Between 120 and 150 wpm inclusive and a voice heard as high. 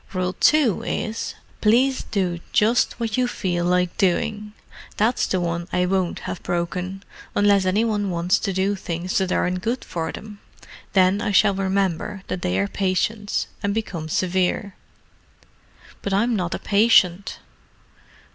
Yes: average, 145 wpm; high, 195 Hz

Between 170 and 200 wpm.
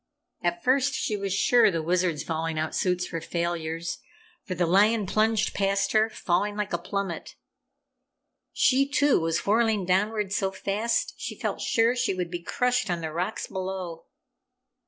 No: average, 160 wpm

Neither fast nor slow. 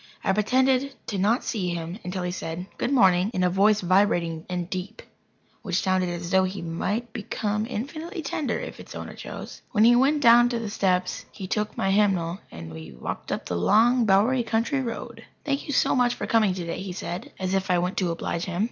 No: fast, 210 wpm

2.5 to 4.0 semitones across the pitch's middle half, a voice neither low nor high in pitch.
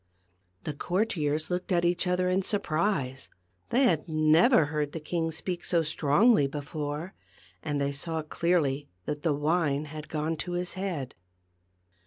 Yes: average, 3.2 semitones; medium, 160 Hz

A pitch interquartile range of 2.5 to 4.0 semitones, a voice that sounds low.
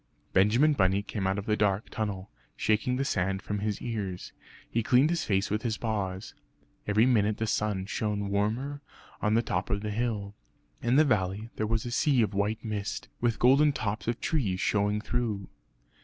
Yes: average, 2.8 semitones; low, 105 Hz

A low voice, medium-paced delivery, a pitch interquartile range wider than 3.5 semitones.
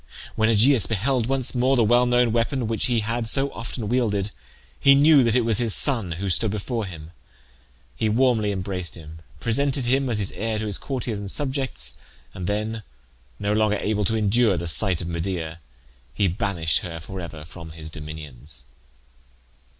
Yes: low, 110 Hz; average, 180 wpm; average, 5.1 semitones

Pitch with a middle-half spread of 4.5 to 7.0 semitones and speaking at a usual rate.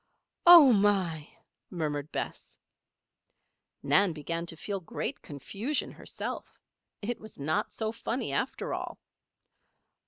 No: wide, 5.6 semitones; slow, 105 wpm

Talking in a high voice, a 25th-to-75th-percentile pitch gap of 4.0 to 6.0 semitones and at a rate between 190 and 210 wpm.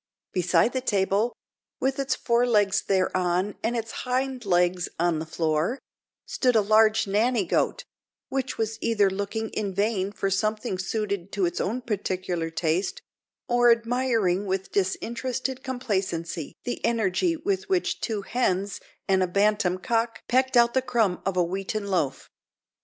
No: high, 210 Hz; average, 4.3 semitones; average, 150 wpm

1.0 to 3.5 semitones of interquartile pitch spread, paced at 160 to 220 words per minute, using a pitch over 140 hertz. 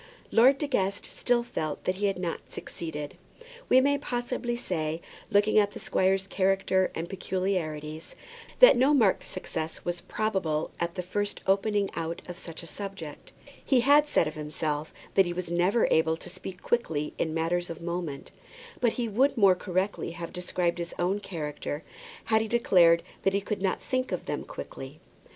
No: average, 4.1 semitones; average, 175 wpm; medium, 185 Hz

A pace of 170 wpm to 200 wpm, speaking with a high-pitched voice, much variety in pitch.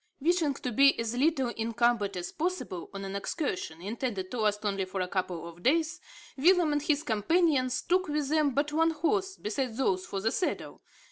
Yes: average, 190 wpm; very high, 255 Hz; wide, 7.6 semitones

